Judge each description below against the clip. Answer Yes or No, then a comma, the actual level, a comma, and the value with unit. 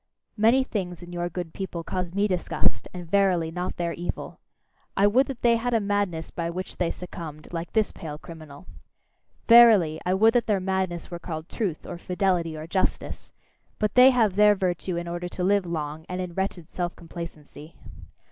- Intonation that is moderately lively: Yes, average, 3.1 semitones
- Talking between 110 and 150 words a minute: No, average, 185 wpm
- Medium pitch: Yes, medium, 180 Hz